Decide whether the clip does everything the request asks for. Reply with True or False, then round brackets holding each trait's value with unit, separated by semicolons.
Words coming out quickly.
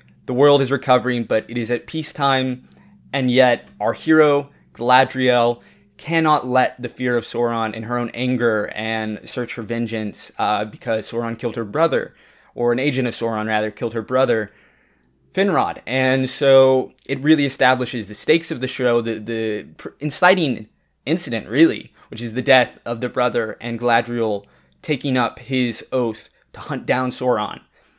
False (165 wpm)